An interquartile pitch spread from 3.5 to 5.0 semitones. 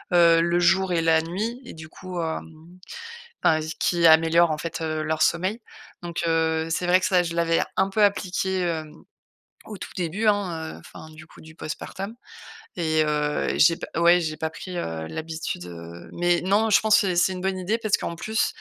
No: average, 2.7 semitones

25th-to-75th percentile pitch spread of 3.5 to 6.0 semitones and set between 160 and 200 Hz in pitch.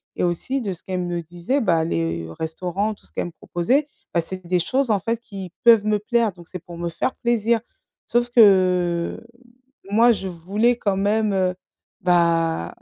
Yes: average, 4.6 semitones; high, 190 Hz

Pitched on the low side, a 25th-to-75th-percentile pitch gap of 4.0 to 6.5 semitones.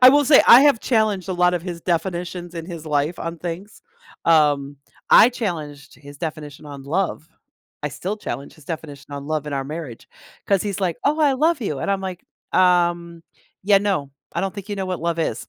No: medium, 175 Hz; average, 4.4 semitones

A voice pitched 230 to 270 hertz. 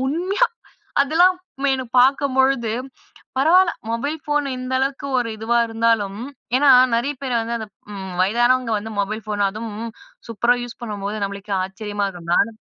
Yes: high, 235 Hz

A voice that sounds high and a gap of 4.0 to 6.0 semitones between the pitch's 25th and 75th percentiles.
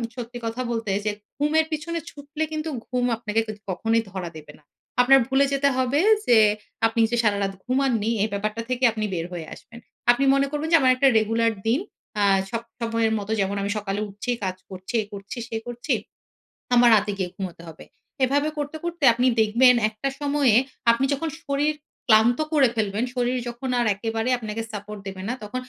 Yes: high, 230 Hz; average, 4.3 semitones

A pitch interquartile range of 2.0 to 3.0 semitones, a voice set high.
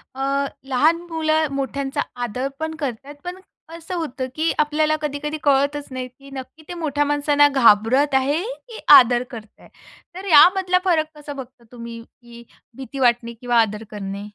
No: average, 3.9 semitones; very high, 275 Hz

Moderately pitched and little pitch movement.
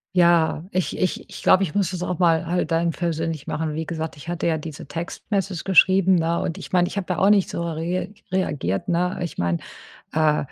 Yes: medium, 170 Hz; narrow, 2.3 semitones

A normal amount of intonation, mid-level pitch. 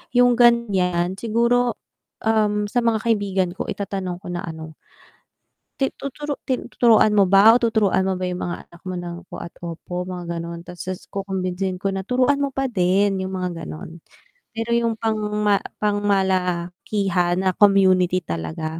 No: average, 4.0 semitones; high, 195 Hz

